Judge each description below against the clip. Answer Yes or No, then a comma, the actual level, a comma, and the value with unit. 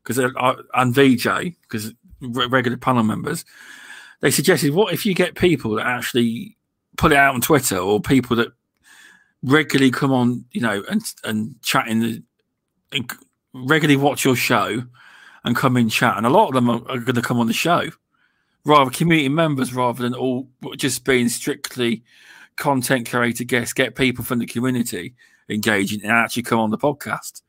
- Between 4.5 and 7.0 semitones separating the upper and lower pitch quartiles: No, average, 2.9 semitones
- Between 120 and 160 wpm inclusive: No, average, 175 wpm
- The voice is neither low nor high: No, low, 125 Hz